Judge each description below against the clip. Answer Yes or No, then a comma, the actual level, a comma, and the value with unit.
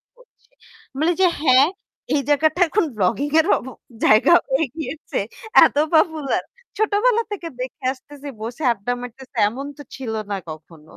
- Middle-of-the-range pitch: No, very high, 280 Hz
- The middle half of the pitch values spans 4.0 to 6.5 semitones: Yes, average, 4.9 semitones